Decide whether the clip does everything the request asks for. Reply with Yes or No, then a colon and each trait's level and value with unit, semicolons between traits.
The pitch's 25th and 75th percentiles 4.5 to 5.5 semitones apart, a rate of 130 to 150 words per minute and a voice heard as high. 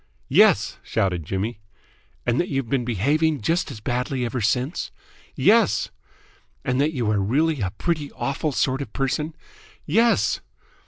No: average, 5.0 semitones; average, 145 wpm; low, 130 Hz